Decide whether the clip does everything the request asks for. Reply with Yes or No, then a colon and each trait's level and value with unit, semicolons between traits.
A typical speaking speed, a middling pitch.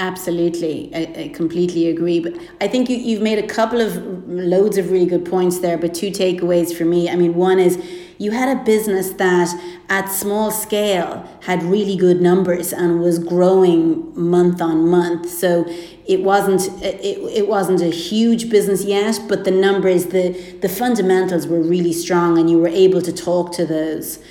Yes: average, 185 wpm; medium, 180 Hz